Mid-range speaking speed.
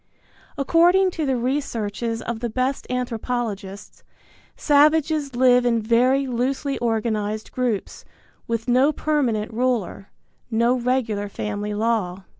No: slow, 110 wpm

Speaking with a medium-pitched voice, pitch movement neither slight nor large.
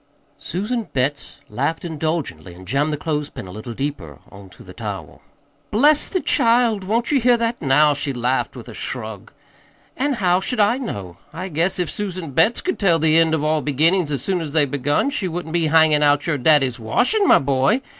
No: medium, 155 Hz; wide, 6.2 semitones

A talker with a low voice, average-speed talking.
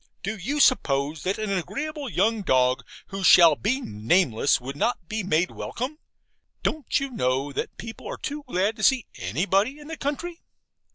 No: high, 200 Hz; average, 170 wpm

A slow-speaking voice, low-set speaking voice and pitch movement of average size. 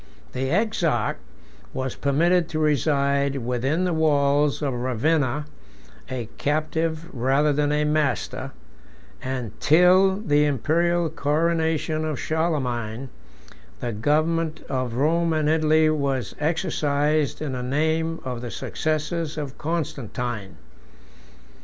No: slow, 110 wpm; medium, 150 Hz; average, 3.3 semitones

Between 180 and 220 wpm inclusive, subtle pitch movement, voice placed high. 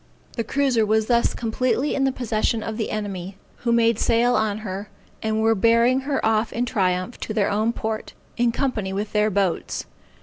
Yes: average, 190 wpm; narrow, 2.2 semitones; high, 220 Hz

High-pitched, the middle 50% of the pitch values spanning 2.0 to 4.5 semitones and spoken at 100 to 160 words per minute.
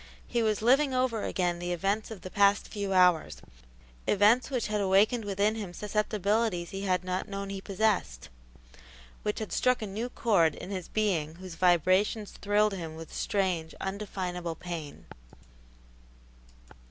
Yes: high, 195 Hz; average, 3.1 semitones; average, 150 wpm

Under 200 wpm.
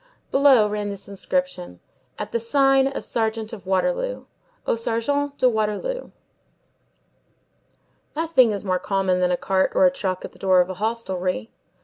Yes: average, 155 wpm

